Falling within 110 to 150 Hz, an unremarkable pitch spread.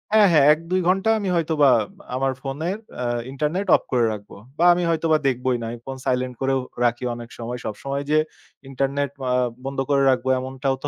Yes: low, 135 Hz; average, 3.8 semitones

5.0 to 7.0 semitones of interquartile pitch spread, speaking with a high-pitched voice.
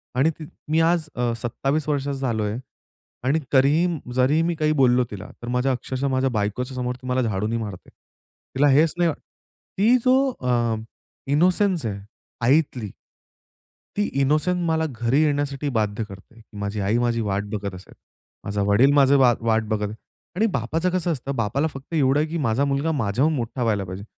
No: average, 5.3 semitones; low, 130 Hz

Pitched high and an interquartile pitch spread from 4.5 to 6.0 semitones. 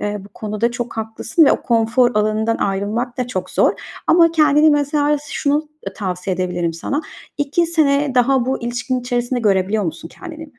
Yes: high, 245 Hz; wide, 5.5 semitones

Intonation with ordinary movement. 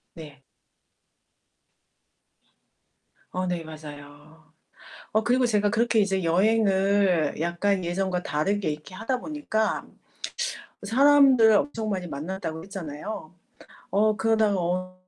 Yes: average, 4.9 semitones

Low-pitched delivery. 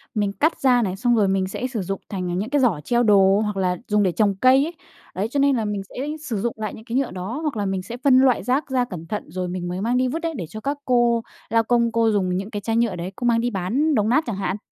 No: high, 220 Hz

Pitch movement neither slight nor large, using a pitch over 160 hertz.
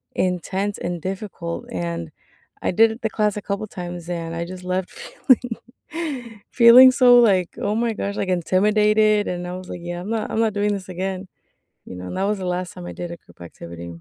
Yes: average, 3.3 semitones; medium, 185 Hz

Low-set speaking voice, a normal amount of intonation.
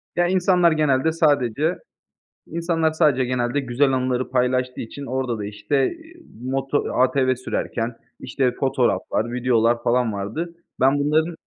Yes: low, 130 Hz; average, 3.9 semitones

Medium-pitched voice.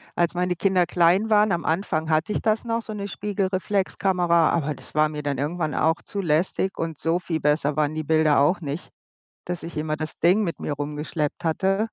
Yes: medium, 170 Hz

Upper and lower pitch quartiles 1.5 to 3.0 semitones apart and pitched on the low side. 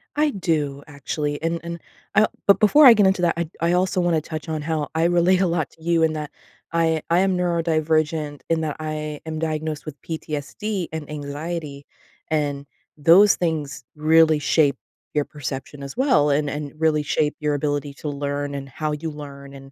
No: narrow, 2.4 semitones; medium, 155 Hz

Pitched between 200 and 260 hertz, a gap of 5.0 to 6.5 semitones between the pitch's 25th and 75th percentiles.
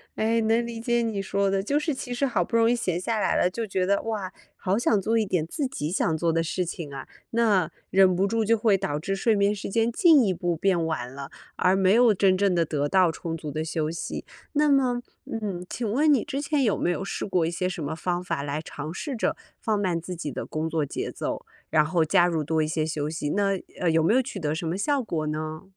No: high, 190 Hz; wide, 5.6 semitones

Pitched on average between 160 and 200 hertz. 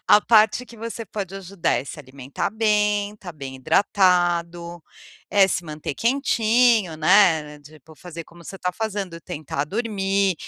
Yes: medium, 185 Hz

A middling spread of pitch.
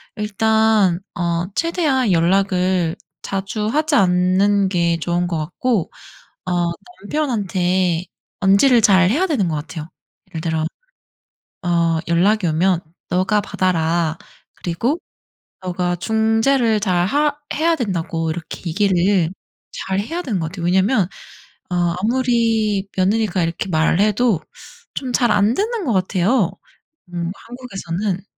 Yes: average, 4.3 semitones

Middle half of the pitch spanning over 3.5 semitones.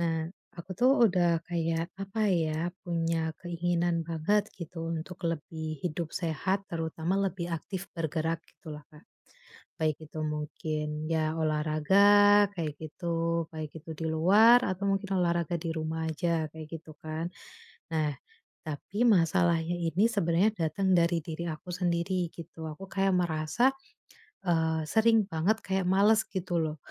No: average, 2.8 semitones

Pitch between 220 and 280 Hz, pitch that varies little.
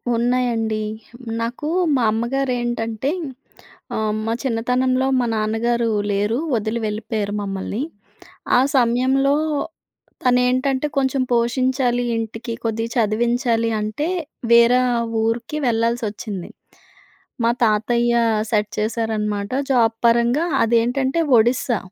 Yes: high, 235 Hz; narrow, 2.1 semitones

